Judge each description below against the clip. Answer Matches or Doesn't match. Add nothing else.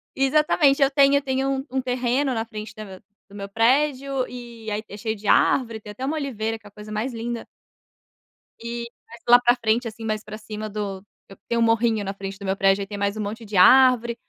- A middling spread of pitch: Matches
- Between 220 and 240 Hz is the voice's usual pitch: Matches